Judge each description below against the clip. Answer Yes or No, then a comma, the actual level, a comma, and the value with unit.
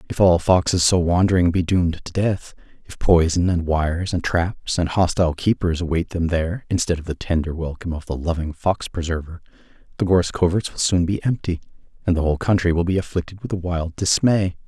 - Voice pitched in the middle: No, very low, 85 Hz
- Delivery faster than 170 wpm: Yes, average, 200 wpm